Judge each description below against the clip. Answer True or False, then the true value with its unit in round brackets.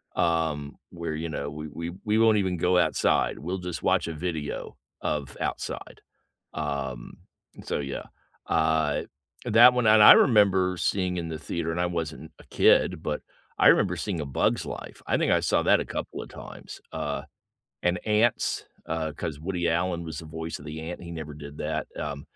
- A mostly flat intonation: False (3.0 semitones)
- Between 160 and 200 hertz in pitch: False (85 Hz)